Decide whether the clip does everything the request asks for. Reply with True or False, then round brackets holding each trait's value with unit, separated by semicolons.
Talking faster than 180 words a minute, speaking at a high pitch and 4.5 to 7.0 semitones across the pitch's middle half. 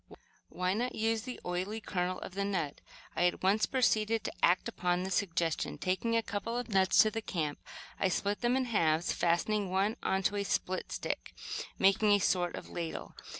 False (190 wpm; 195 Hz; 3.4 semitones)